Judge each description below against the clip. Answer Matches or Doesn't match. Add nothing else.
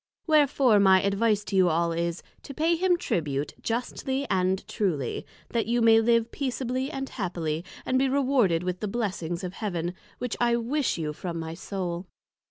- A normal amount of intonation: Doesn't match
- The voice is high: Matches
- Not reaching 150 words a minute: Doesn't match